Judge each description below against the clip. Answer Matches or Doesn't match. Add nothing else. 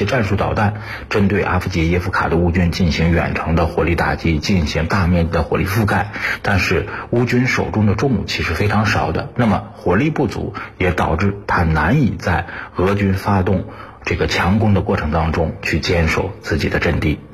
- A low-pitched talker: Matches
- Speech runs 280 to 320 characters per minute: Matches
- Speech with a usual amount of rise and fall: Matches